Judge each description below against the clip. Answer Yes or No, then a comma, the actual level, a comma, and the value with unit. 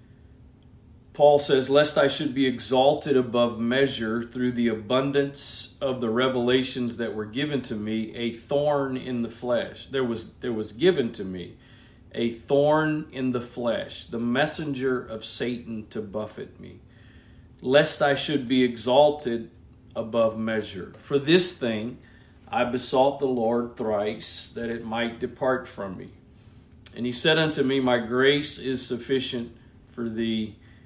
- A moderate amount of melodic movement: Yes, average, 3.0 semitones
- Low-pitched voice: Yes, low, 125 Hz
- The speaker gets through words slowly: No, average, 150 wpm